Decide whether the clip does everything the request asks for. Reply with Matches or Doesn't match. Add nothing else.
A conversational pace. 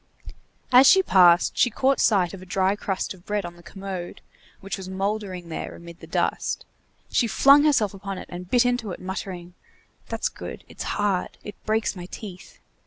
Matches